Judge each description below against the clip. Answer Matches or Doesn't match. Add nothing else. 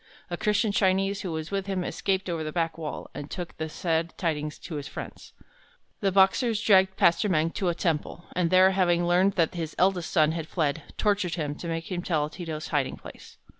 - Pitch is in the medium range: Matches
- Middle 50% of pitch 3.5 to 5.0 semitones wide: Doesn't match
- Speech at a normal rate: Doesn't match